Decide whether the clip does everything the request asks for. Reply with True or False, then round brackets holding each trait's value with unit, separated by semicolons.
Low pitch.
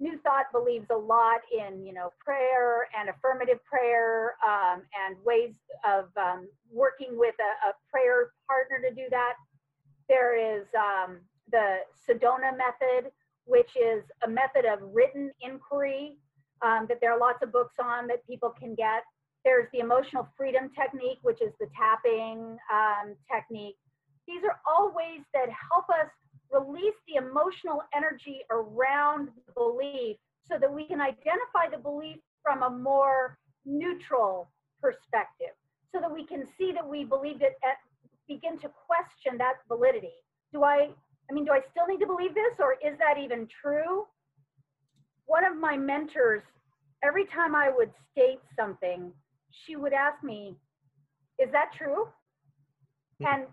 False (260 Hz)